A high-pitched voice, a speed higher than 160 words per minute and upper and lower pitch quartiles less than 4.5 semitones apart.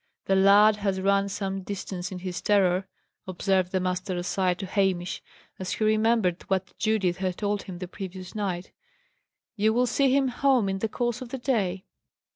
Yes: high, 195 Hz; average, 180 wpm; average, 2.7 semitones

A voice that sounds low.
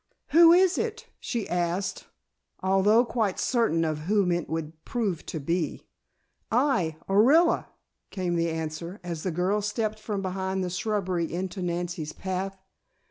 No: high, 190 Hz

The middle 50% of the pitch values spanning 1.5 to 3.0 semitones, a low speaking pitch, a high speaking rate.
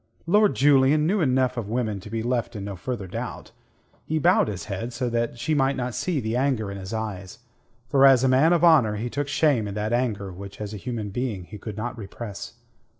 No: average, 4.3 semitones; low, 120 Hz; fast, 225 wpm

